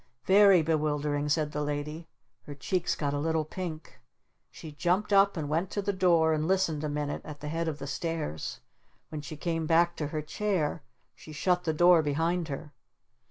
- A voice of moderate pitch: Yes, medium, 160 Hz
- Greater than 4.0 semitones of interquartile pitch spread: No, average, 2.7 semitones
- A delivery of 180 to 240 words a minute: Yes, average, 190 wpm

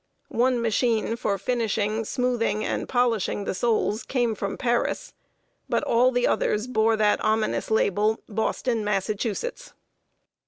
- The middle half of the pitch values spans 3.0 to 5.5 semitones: No, narrow, 2.5 semitones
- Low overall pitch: No, high, 225 Hz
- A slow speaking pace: Yes, slow, 125 wpm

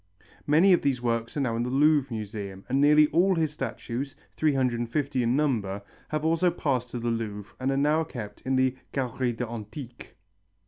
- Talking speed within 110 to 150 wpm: No, average, 185 wpm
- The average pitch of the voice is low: Yes, low, 130 Hz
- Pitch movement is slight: No, average, 4.2 semitones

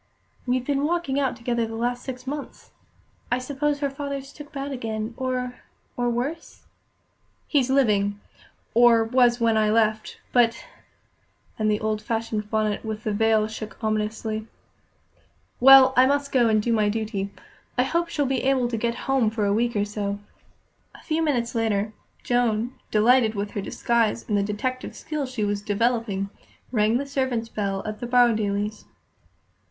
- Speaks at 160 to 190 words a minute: Yes, average, 165 wpm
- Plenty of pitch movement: No, average, 3.2 semitones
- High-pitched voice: Yes, high, 235 Hz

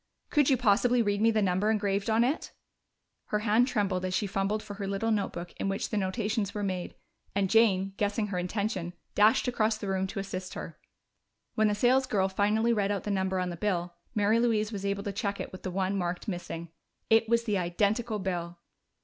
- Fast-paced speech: Yes, fast, 210 wpm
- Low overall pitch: No, high, 205 Hz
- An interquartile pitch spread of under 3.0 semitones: Yes, narrow, 2.5 semitones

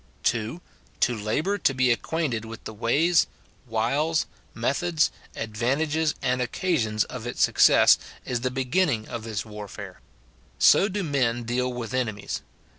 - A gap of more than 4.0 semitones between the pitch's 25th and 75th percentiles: Yes, average, 5.2 semitones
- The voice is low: Yes, low, 125 Hz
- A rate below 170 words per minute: Yes, average, 140 wpm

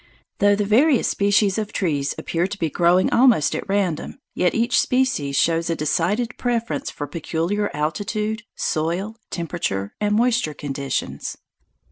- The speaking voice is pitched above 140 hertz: Yes, high, 190 Hz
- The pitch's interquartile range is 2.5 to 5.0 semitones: No, wide, 5.4 semitones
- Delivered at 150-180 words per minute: No, average, 140 wpm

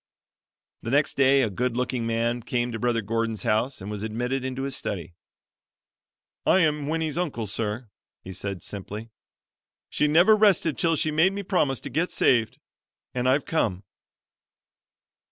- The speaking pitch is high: No, low, 125 Hz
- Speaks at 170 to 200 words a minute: No, average, 155 wpm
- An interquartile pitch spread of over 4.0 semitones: Yes, average, 5.1 semitones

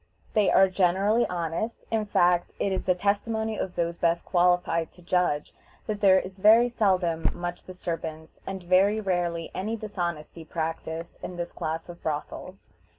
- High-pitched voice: No, medium, 180 Hz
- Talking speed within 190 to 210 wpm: No, average, 155 wpm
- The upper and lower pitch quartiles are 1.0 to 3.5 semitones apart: Yes, average, 2.9 semitones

